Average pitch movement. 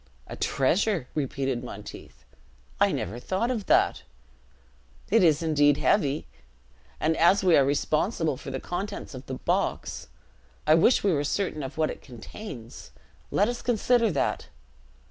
No: wide, 6.6 semitones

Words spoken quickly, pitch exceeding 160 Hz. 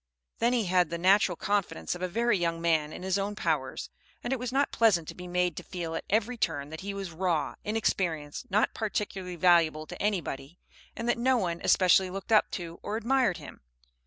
Yes: fast, 210 wpm; medium, 185 Hz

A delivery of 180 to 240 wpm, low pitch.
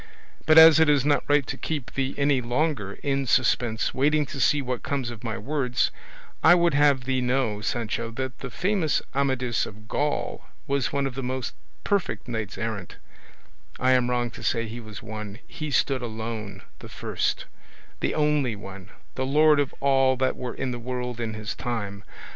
Yes: average, 185 wpm; low, 130 Hz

